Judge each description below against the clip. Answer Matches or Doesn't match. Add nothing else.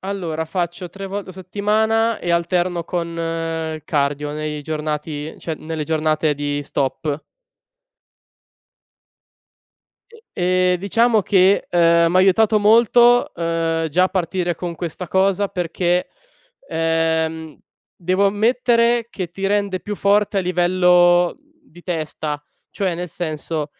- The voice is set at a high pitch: Doesn't match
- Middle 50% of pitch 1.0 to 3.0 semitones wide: Doesn't match